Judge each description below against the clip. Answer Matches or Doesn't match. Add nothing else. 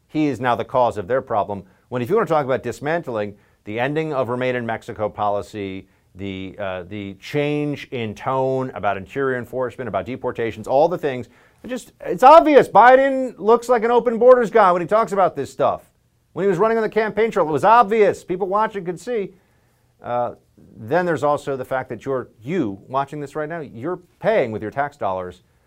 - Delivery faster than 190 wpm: Matches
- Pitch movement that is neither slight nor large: Doesn't match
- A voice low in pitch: Matches